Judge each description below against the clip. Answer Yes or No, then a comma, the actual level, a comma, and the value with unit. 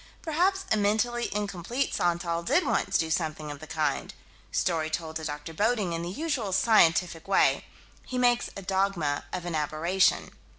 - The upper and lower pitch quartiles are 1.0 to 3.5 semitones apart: No, wide, 5.5 semitones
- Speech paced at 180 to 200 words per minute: No, average, 165 wpm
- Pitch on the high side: No, medium, 180 Hz